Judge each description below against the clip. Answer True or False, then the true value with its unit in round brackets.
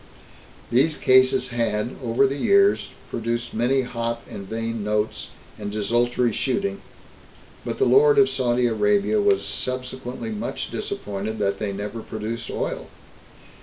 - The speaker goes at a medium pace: False (130 wpm)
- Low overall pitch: True (115 Hz)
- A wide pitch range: False (3.3 semitones)